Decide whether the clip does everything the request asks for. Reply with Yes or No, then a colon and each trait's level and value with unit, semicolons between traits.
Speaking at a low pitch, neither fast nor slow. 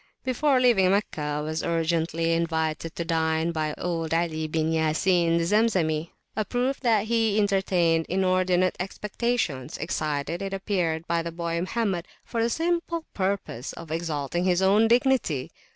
No: medium, 175 Hz; average, 150 wpm